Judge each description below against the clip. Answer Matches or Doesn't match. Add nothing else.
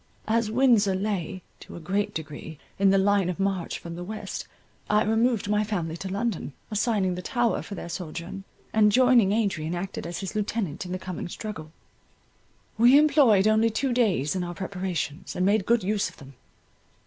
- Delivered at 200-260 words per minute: Doesn't match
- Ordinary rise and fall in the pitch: Matches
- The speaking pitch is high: Matches